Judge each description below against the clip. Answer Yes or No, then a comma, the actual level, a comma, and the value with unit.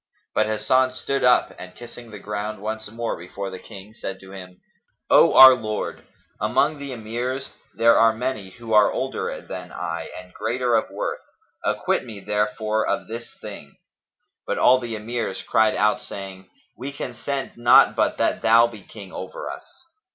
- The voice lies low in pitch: Yes, low, 110 Hz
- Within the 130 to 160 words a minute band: No, average, 175 wpm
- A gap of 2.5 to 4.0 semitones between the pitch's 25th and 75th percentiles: Yes, average, 2.8 semitones